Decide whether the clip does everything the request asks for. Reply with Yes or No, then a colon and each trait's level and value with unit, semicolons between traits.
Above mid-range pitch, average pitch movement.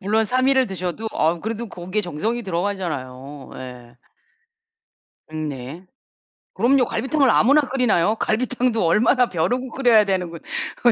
No: high, 210 Hz; wide, 6.6 semitones